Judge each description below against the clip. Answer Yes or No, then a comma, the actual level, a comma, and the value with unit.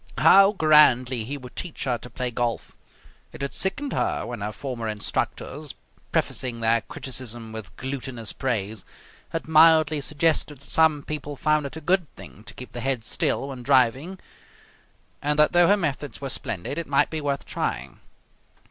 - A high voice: No, medium, 140 Hz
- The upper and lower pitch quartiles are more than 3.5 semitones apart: Yes, average, 4.2 semitones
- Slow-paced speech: No, average, 170 wpm